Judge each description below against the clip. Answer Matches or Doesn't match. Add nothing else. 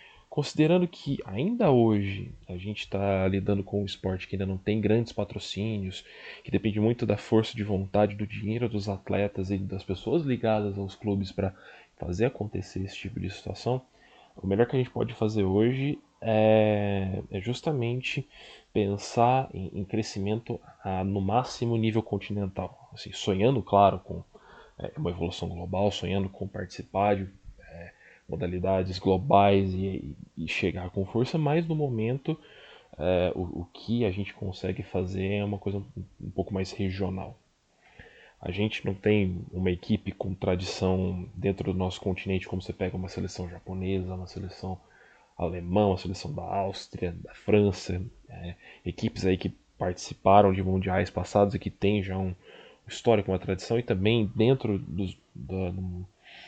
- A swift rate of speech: Doesn't match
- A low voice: Matches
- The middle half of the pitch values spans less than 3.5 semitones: Matches